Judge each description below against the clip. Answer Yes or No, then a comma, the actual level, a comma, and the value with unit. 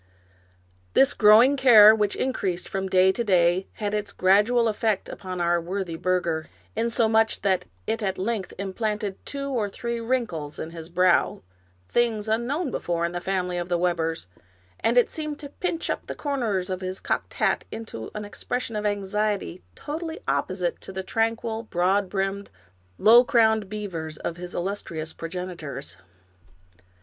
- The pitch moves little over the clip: No, average, 4.0 semitones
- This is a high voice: Yes, high, 200 Hz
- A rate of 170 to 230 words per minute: No, average, 155 wpm